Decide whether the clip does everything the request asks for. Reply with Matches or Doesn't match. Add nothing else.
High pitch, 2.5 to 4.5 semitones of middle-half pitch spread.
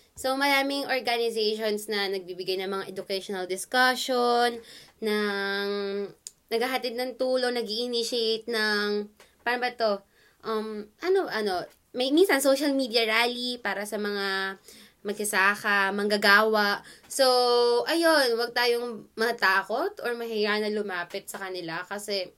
Matches